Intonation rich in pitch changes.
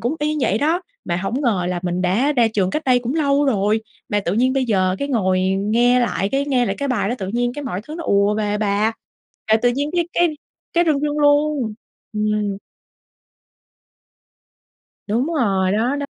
Yes: wide, 5.9 semitones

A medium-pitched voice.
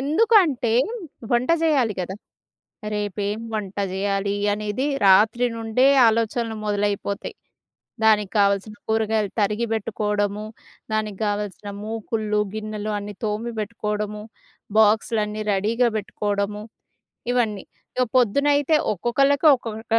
No: high, 215 Hz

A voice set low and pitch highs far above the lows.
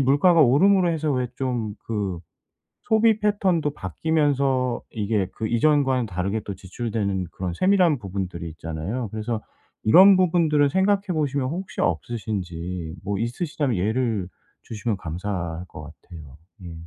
Yes: low, 120 Hz; wide, 8.2 semitones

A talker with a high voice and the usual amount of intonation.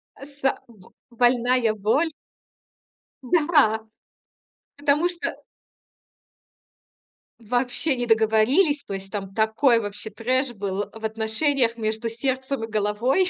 Yes: high, 235 Hz; average, 3.9 semitones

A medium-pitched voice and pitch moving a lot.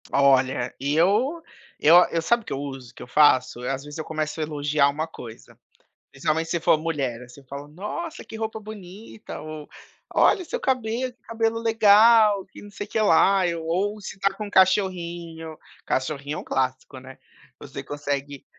Yes: medium, 160 Hz; wide, 6.7 semitones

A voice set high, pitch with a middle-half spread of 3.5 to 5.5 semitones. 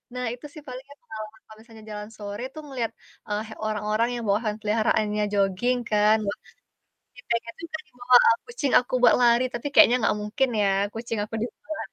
No: high, 225 Hz; average, 2.9 semitones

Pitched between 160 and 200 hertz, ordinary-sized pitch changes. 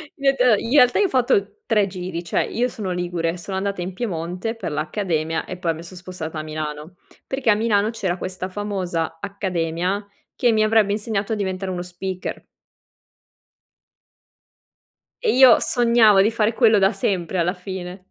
Yes: high, 190 Hz; average, 3.7 semitones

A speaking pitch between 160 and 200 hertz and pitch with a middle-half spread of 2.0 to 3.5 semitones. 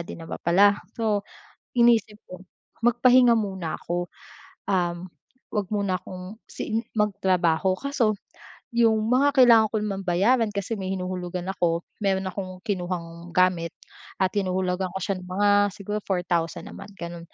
Yes: high, 190 Hz; average, 2.9 semitones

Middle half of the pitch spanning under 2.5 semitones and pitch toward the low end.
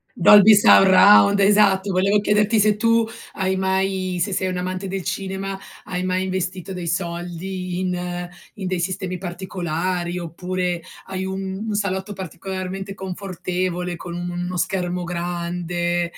No: narrow, 1.5 semitones; medium, 185 Hz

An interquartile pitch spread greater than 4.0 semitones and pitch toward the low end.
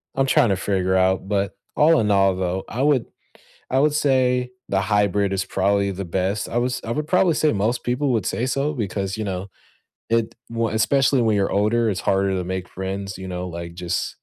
Yes: average, 4.6 semitones; low, 100 Hz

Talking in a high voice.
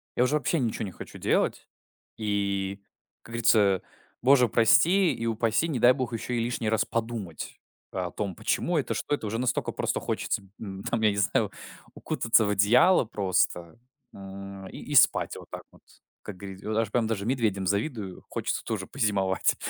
No: low, 110 Hz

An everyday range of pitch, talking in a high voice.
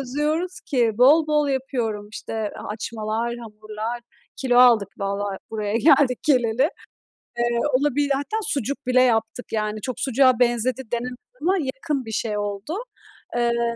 Yes: average, 3.6 semitones; high, 240 Hz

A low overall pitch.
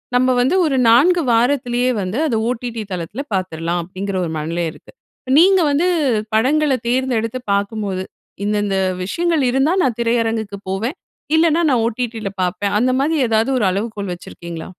No: high, 230 Hz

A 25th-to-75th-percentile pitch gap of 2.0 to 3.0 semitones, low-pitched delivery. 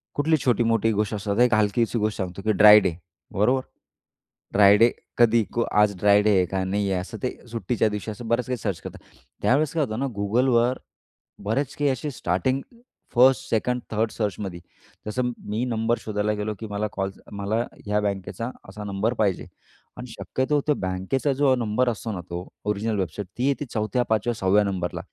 No: average, 3.4 semitones; low, 110 Hz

